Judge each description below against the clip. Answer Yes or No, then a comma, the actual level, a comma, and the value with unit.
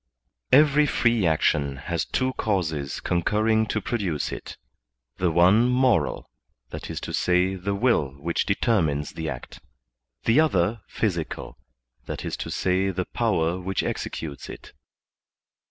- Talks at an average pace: No, slow, 110 wpm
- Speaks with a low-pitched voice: Yes, very low, 95 Hz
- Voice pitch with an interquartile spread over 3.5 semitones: Yes, wide, 5.6 semitones